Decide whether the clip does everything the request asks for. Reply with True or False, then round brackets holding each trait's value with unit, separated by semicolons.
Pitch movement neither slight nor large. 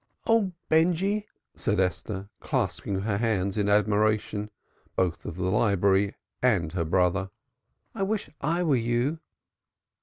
False (6.9 semitones)